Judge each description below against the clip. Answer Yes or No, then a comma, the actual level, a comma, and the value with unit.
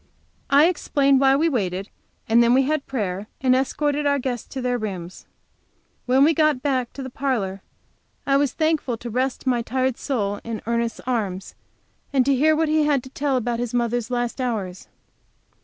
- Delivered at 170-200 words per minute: Yes, average, 190 wpm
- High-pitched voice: Yes, very high, 255 Hz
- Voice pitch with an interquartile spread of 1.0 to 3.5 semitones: Yes, average, 3.2 semitones